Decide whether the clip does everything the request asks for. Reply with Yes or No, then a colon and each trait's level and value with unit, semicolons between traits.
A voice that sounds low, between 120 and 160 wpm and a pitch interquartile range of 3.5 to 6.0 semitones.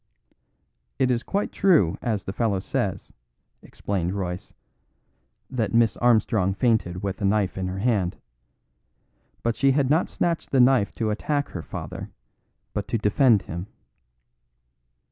Yes: low, 110 Hz; average, 140 wpm; average, 4.6 semitones